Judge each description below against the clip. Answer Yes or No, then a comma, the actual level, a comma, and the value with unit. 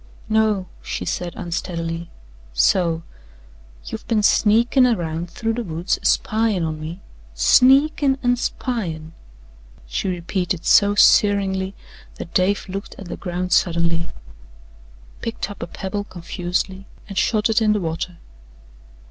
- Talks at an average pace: No, slow, 130 wpm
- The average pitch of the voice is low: No, high, 190 Hz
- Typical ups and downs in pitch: Yes, average, 4.1 semitones